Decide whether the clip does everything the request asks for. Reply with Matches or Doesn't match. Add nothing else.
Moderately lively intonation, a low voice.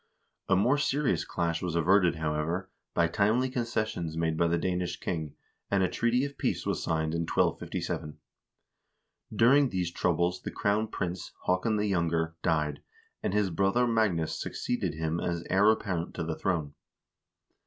Matches